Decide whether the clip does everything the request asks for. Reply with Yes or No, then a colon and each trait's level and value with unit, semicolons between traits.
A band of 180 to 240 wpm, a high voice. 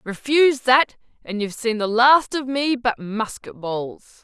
No: average, 170 wpm; high, 240 Hz